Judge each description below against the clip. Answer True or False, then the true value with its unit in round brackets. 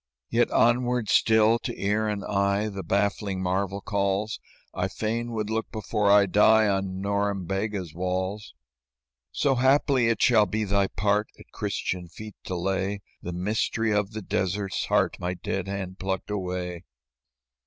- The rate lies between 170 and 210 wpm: False (150 wpm)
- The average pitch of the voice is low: True (100 Hz)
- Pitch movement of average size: False (2.3 semitones)